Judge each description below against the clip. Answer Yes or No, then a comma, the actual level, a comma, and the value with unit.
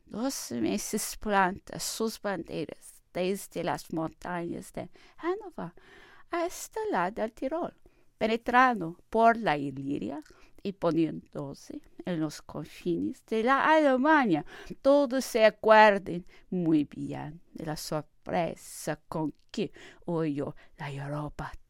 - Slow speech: Yes, slow, 110 wpm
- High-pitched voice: Yes, high, 205 Hz